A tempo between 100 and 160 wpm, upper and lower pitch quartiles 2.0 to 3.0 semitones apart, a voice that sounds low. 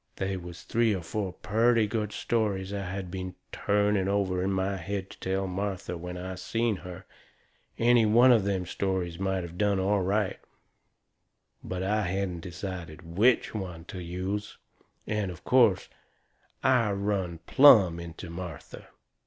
Yes: average, 155 wpm; narrow, 2.4 semitones; very low, 95 Hz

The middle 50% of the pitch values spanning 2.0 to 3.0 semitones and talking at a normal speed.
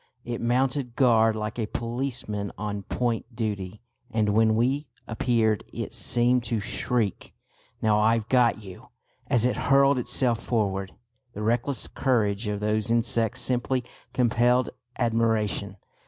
No: narrow, 2.4 semitones; slow, 130 wpm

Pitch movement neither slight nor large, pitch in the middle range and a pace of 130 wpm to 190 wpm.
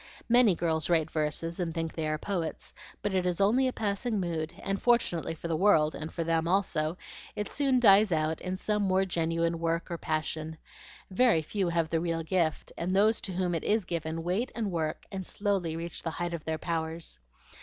No: average, 3.4 semitones; medium, 170 Hz; fast, 205 wpm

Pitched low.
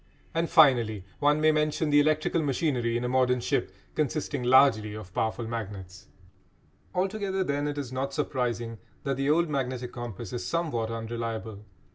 Yes: low, 130 Hz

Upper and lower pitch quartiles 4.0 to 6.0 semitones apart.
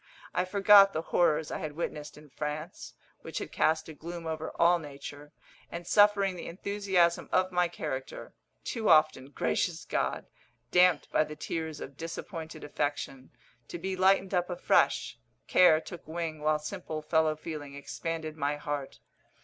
No: average, 2.9 semitones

